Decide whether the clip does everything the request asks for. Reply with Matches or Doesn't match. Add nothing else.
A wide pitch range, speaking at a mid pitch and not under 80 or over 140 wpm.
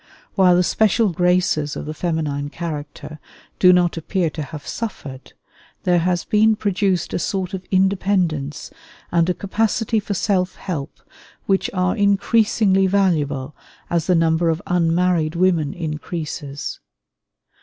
Doesn't match